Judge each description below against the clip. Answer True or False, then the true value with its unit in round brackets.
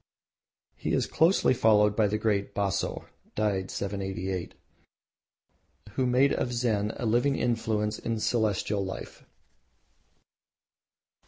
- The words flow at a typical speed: False (100 wpm)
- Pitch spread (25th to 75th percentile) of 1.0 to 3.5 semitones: True (3.1 semitones)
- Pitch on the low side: True (105 Hz)